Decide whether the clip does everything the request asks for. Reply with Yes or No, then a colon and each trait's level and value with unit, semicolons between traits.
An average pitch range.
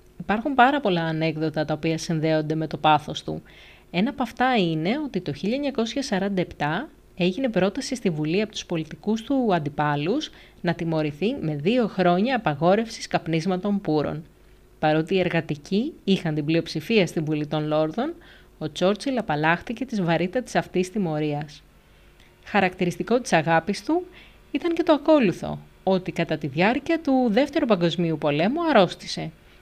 No: wide, 6.5 semitones